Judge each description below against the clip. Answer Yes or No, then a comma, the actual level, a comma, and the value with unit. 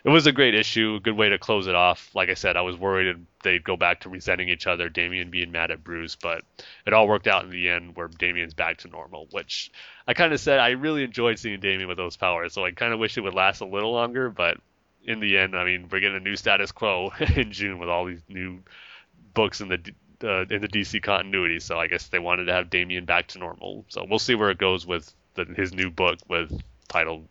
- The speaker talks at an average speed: No, fast, 255 wpm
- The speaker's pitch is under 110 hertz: Yes, very low, 95 Hz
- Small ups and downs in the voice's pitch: No, average, 3.4 semitones